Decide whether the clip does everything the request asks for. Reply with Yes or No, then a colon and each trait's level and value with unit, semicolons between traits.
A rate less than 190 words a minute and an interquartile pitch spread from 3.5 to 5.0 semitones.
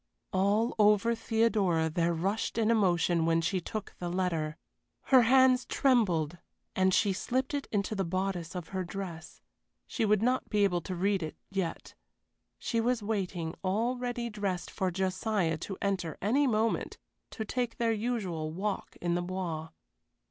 Yes: average, 160 wpm; average, 4.4 semitones